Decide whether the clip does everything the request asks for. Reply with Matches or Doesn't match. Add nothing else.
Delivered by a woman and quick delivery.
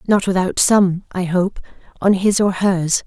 Doesn't match